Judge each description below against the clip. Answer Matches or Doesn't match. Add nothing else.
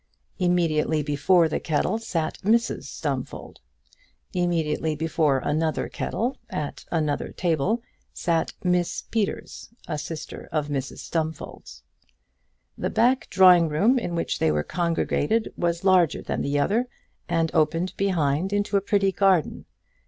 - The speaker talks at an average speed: Doesn't match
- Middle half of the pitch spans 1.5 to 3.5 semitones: Doesn't match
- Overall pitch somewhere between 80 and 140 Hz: Doesn't match